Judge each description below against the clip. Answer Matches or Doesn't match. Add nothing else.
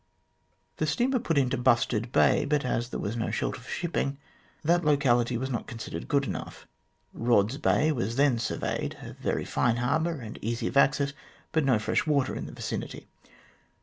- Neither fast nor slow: Matches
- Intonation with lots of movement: Doesn't match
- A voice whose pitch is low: Matches